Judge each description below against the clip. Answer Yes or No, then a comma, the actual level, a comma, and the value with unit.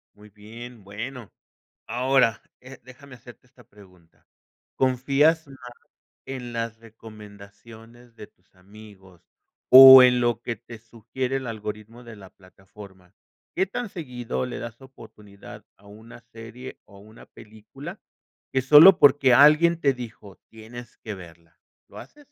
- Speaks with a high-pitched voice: No, low, 115 Hz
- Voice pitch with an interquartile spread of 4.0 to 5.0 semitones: No, average, 3.6 semitones